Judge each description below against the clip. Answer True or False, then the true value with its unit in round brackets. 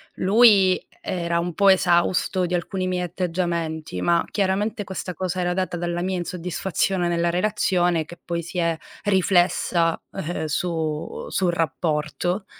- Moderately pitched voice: True (175 Hz)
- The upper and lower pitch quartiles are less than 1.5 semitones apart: False (1.8 semitones)